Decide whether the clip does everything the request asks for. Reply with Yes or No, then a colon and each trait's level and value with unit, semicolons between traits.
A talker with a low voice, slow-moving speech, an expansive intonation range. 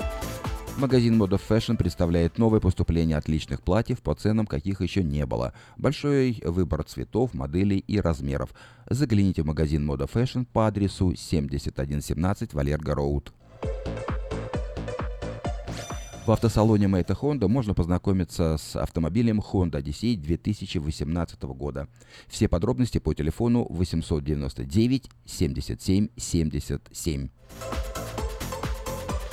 Yes: very low, 90 Hz; slow, 95 wpm; wide, 6.2 semitones